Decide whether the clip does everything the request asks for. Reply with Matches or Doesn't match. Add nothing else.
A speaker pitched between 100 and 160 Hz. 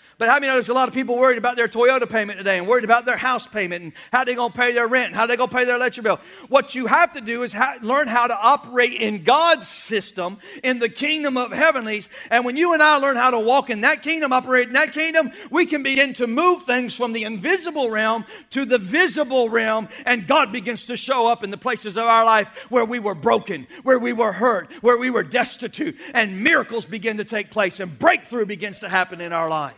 Doesn't match